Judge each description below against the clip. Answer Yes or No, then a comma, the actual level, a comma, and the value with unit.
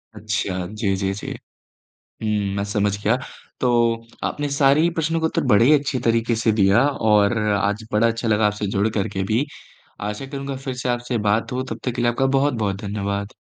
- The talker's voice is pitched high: No, low, 110 Hz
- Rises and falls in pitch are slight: No, average, 3.8 semitones